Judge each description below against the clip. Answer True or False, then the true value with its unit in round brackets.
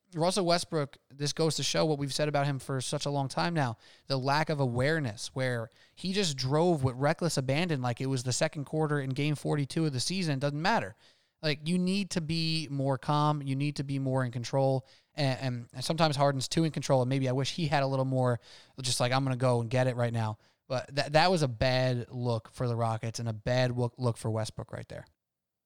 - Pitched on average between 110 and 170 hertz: True (135 Hz)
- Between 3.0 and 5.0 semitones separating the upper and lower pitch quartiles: True (3.4 semitones)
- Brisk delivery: True (240 wpm)